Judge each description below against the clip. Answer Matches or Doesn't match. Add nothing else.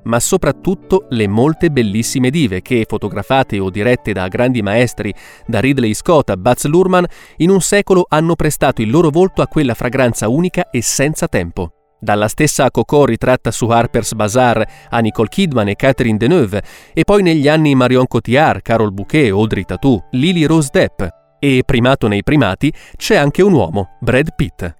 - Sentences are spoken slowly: Doesn't match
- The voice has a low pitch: Matches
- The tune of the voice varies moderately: Doesn't match